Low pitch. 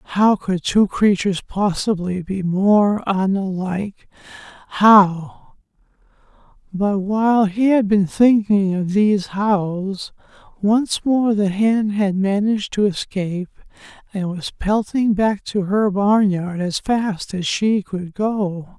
No: high, 200 Hz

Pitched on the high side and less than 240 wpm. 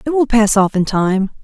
No: high, 220 Hz; fast, 250 wpm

